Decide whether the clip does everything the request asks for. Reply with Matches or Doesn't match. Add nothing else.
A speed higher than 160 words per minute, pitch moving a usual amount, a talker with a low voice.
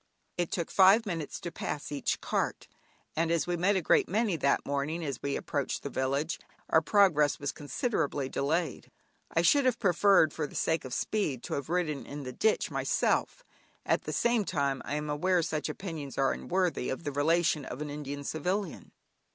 Doesn't match